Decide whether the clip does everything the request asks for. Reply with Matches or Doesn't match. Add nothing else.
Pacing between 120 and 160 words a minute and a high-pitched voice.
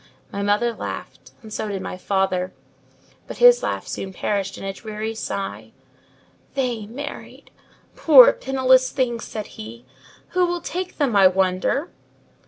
Matches